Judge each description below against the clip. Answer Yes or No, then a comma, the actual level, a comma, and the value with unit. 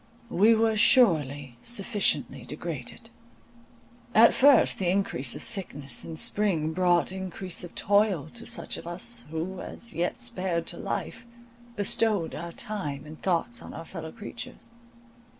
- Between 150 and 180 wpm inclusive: No, average, 140 wpm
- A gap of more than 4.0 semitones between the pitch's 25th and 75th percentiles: Yes, average, 5.2 semitones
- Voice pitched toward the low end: No, medium, 185 Hz